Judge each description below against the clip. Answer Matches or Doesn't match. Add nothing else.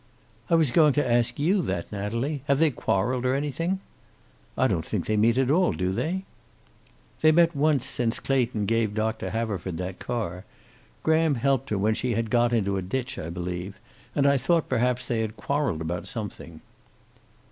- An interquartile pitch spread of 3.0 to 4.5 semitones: Doesn't match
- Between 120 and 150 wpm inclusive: Doesn't match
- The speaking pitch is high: Doesn't match